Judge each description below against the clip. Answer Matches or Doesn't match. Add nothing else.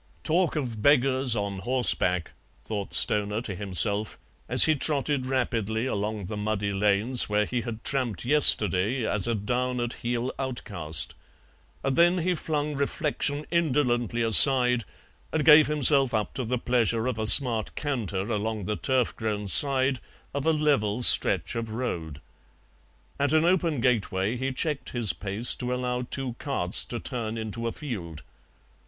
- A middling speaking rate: Matches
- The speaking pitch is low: Matches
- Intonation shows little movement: Doesn't match